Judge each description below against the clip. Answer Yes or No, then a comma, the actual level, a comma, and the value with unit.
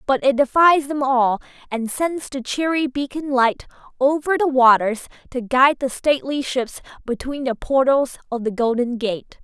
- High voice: Yes, very high, 265 Hz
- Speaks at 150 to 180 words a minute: Yes, average, 165 wpm